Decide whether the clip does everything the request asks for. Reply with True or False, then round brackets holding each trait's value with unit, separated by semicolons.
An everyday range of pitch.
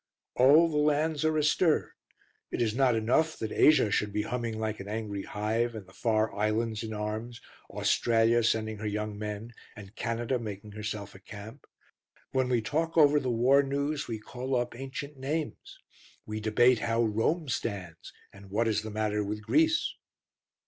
True (4.0 semitones)